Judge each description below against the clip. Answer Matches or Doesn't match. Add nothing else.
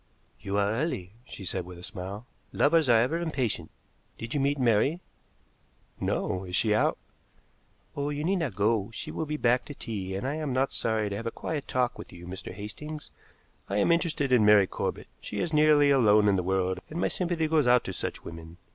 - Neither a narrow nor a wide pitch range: Doesn't match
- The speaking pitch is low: Matches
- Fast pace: Matches